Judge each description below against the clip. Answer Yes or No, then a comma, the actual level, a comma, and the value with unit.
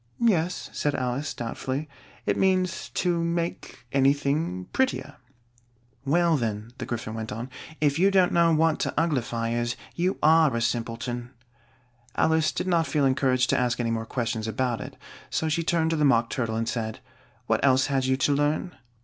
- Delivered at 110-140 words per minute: No, average, 175 wpm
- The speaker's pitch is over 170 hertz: No, medium, 140 Hz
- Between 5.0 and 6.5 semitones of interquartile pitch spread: Yes, wide, 5.4 semitones